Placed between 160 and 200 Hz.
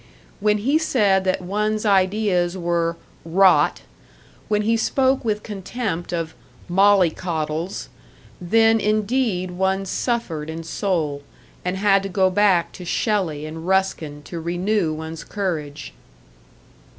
Yes: high, 190 Hz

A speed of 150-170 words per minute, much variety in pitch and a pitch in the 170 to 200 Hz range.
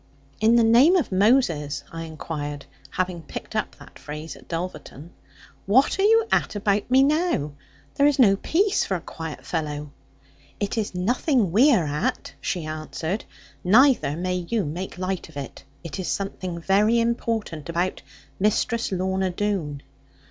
Yes: average, 155 wpm; wide, 6.1 semitones; high, 190 Hz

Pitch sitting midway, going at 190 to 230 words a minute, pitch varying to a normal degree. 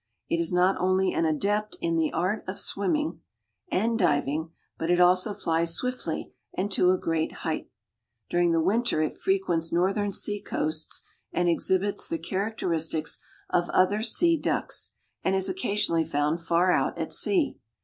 No: medium, 180 Hz; average, 160 wpm; average, 3.7 semitones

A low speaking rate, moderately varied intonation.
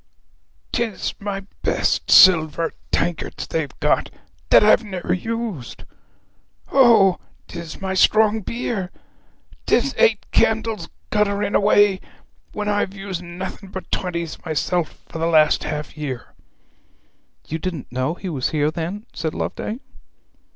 Yes: slow, 125 wpm; average, 4.3 semitones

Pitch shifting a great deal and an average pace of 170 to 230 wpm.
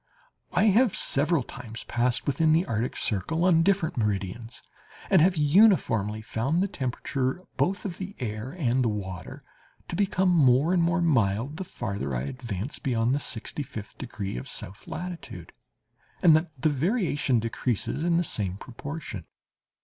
No: wide, 7.3 semitones; average, 155 wpm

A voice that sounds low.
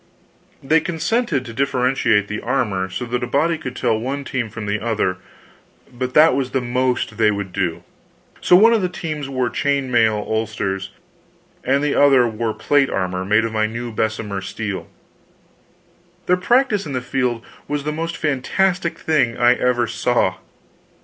Yes: low, 125 Hz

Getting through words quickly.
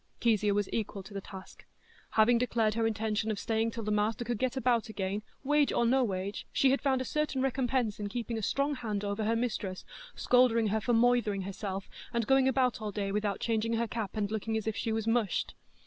Yes: fast, 220 wpm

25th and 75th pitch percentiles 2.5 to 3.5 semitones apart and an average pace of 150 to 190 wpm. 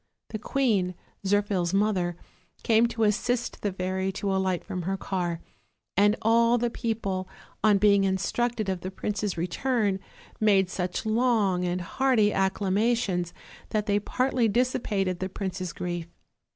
No: average, 3.1 semitones; average, 140 wpm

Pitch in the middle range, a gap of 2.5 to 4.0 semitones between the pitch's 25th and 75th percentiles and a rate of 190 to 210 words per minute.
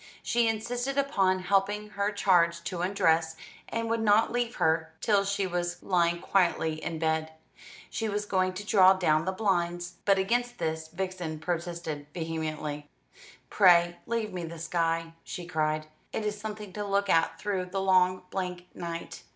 No: medium, 180 Hz; average, 3.6 semitones; average, 160 wpm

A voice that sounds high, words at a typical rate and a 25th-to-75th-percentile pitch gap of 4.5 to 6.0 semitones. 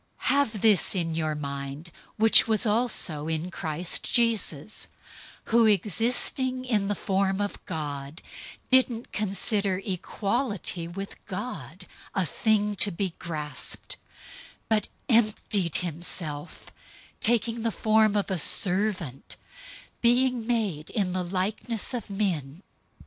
No: high, 195 Hz; slow, 120 wpm; average, 4.8 semitones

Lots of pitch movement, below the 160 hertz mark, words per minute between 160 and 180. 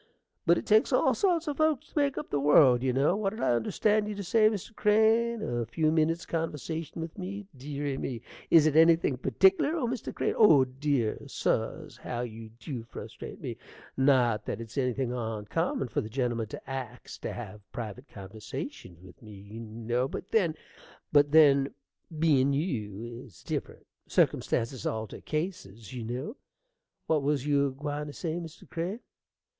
Yes: wide, 6.2 semitones; medium, 140 Hz; average, 170 wpm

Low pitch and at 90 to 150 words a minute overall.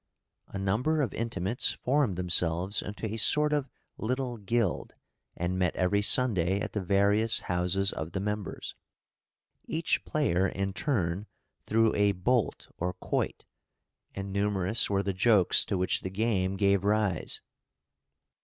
Yes: low, 100 Hz; average, 140 wpm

